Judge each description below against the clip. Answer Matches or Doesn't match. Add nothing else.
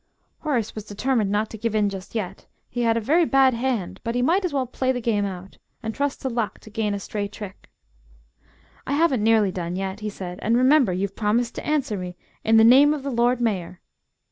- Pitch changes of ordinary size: Matches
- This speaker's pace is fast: Matches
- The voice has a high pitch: Matches